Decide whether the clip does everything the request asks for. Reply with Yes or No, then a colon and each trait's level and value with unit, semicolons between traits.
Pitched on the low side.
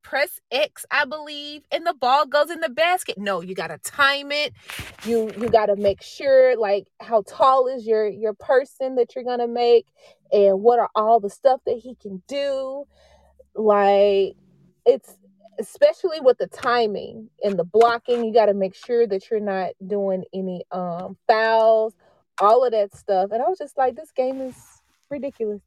No: high, 235 Hz